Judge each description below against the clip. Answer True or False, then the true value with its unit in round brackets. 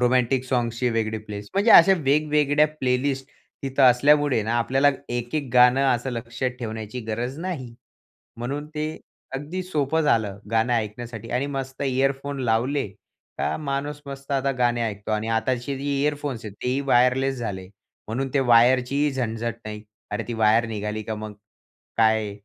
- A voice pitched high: False (125 Hz)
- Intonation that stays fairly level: False (3.4 semitones)